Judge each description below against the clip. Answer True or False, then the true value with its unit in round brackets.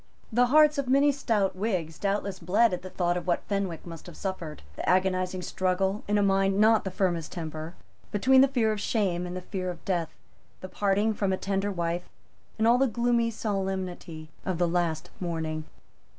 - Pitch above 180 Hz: True (190 Hz)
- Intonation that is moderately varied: True (3.4 semitones)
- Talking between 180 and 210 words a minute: True (195 wpm)